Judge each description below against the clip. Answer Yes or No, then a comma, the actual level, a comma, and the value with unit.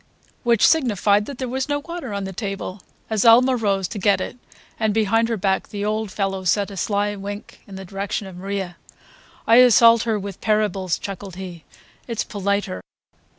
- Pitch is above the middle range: Yes, high, 205 Hz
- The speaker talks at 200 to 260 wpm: No, average, 180 wpm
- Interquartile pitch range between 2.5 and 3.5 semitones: Yes, average, 2.8 semitones